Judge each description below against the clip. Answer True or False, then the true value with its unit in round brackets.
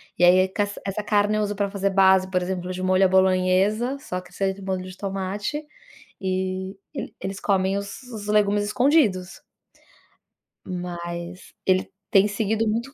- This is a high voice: True (195 Hz)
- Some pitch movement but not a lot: False (1.9 semitones)